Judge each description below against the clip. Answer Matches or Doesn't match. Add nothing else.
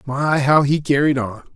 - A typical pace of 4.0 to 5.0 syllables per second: Matches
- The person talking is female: Doesn't match